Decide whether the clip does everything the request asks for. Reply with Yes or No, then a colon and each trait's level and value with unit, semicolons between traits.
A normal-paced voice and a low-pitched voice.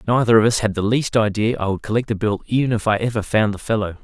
No: fast, 285 wpm; low, 110 Hz